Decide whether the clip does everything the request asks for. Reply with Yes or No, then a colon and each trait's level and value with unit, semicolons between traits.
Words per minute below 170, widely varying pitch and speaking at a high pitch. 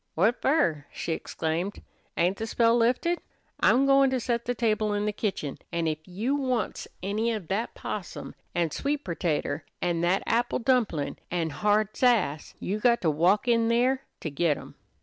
No: average, 175 wpm; wide, 5.9 semitones; high, 210 Hz